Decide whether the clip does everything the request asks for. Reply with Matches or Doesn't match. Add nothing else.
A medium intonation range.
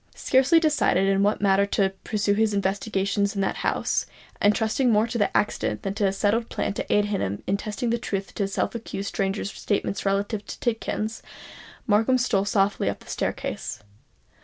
Doesn't match